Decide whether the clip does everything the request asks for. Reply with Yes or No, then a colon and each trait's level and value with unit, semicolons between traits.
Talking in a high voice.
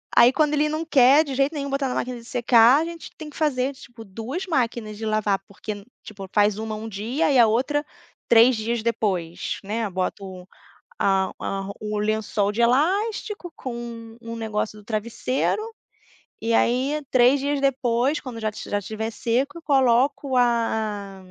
Yes: high, 235 Hz